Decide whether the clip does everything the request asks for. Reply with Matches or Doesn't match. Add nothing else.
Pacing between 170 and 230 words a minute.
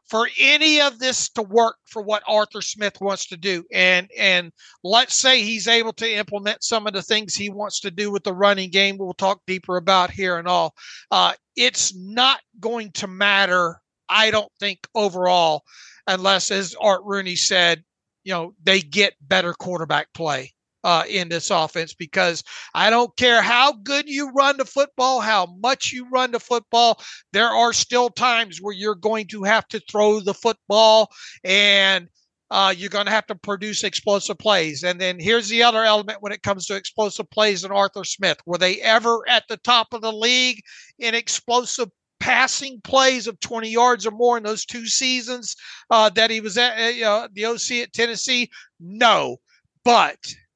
Matches